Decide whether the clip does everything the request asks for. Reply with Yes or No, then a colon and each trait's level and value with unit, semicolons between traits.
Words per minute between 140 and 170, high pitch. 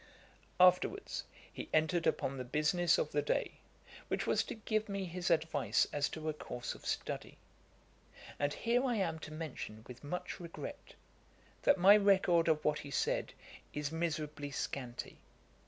No: average, 160 wpm; medium, 160 Hz